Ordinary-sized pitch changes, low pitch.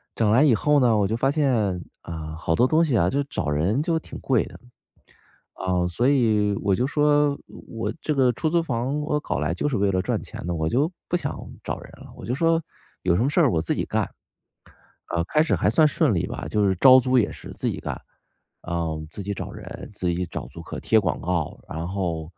No: wide, 8.3 semitones; low, 110 Hz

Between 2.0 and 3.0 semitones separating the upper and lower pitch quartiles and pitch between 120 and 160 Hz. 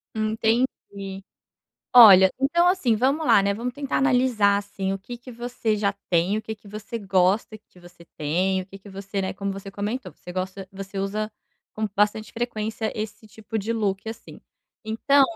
No: average, 2.7 semitones; high, 210 Hz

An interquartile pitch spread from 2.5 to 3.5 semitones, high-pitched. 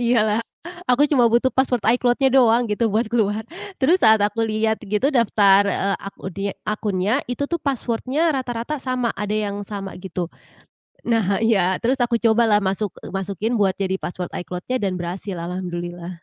No: average, 3.9 semitones; high, 215 Hz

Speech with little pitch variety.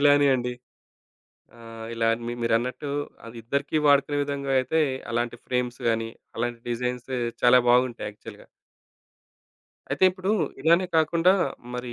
No: average, 3.3 semitones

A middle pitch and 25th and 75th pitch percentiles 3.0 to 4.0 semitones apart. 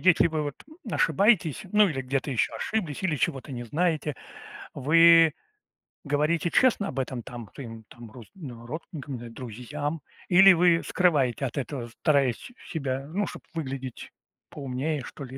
No: medium, 145 Hz; average, 4.4 semitones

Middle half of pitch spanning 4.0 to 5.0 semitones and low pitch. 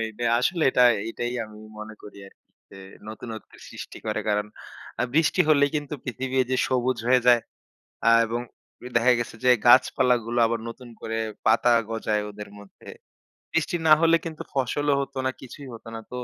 No: average, 2.8 semitones; low, 120 Hz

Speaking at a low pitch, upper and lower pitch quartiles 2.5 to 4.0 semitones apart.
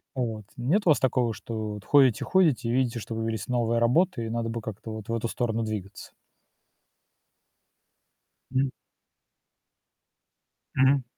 Yes: low, 115 Hz; average, 2.8 semitones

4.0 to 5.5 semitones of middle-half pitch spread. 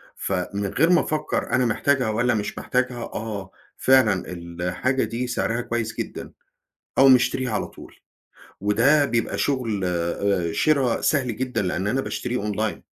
Yes: average, 4.4 semitones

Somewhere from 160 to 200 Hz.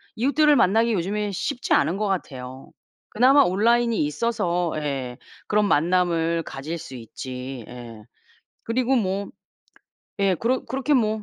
Yes: high, 190 Hz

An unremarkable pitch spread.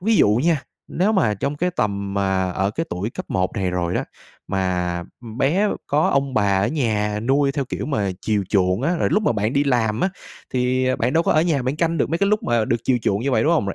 No: wide, 7.1 semitones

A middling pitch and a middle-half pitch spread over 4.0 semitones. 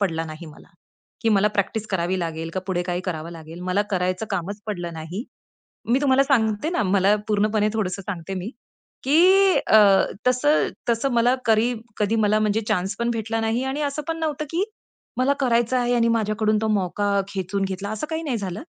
No: high, 215 Hz; average, 4.7 semitones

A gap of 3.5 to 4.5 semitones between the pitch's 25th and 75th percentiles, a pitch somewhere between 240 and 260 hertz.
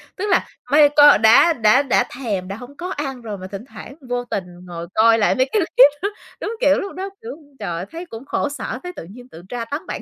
No: average, 5.3 semitones; very high, 250 Hz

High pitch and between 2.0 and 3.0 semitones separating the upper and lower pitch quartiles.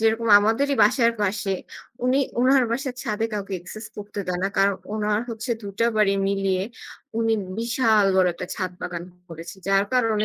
Yes: high, 210 Hz; average, 2.7 semitones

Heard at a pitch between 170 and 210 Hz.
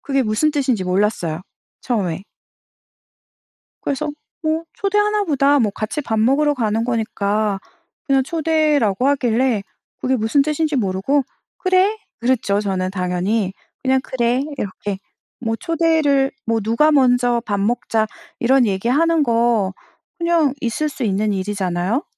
No: high, 240 Hz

